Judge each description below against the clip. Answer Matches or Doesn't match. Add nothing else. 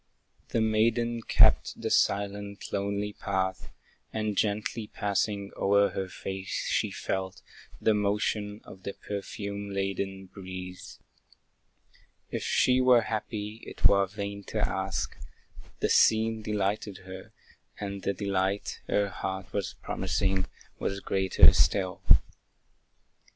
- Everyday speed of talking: Doesn't match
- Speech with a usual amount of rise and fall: Doesn't match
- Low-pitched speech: Matches